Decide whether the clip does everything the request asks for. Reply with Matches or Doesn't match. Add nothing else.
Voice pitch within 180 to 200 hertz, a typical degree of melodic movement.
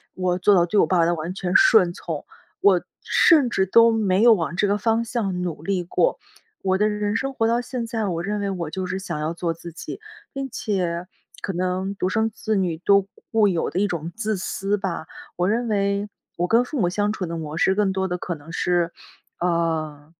Matches